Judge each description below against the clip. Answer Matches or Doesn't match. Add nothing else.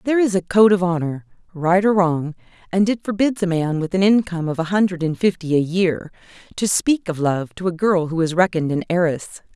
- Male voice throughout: Doesn't match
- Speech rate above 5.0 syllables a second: Matches